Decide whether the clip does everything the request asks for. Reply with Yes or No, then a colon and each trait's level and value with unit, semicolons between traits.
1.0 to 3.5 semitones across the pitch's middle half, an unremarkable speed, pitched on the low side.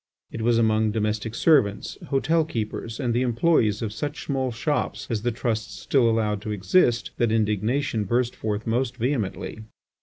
Yes: average, 3.0 semitones; average, 160 wpm; low, 115 Hz